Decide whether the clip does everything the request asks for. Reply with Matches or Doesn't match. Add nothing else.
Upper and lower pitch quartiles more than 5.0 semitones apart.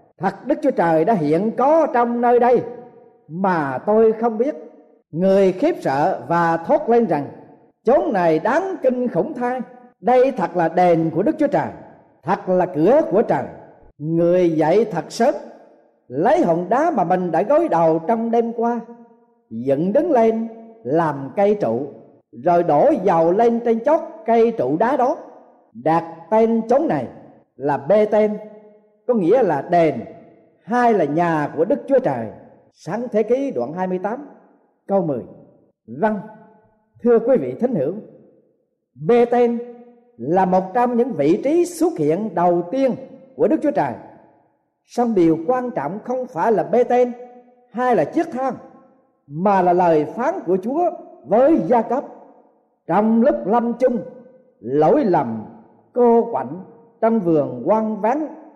Matches